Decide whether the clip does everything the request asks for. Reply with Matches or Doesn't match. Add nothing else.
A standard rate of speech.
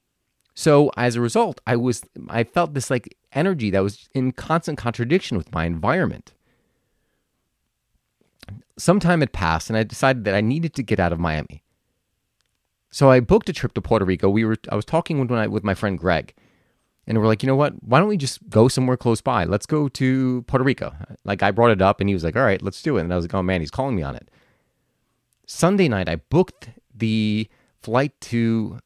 Doesn't match